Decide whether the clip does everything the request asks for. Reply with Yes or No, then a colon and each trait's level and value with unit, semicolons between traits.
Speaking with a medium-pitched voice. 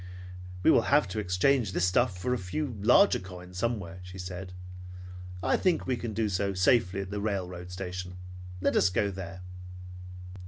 No: very low, 95 Hz